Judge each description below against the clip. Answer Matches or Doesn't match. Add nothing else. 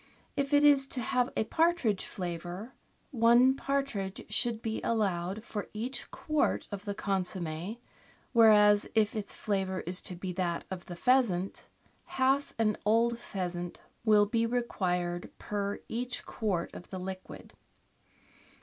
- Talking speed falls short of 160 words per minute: Matches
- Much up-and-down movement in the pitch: Doesn't match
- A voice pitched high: Matches